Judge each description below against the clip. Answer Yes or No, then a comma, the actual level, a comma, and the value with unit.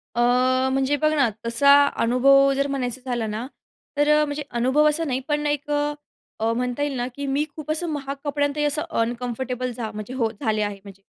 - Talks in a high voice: Yes, very high, 270 Hz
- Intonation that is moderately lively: Yes, average, 3.5 semitones